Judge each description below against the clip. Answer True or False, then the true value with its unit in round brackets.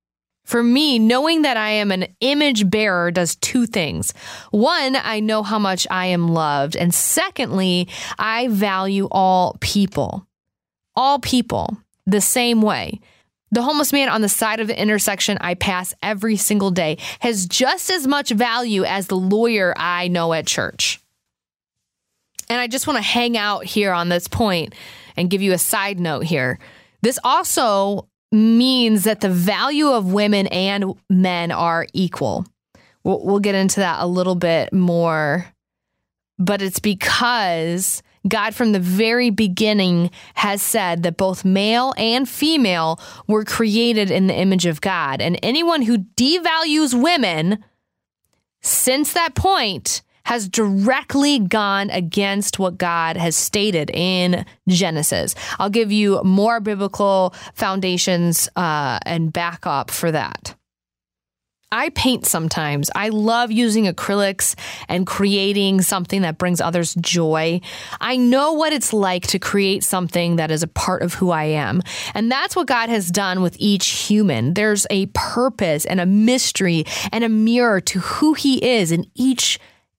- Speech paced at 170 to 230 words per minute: False (150 wpm)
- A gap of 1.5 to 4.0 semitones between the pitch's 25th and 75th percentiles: False (4.5 semitones)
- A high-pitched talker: True (200 Hz)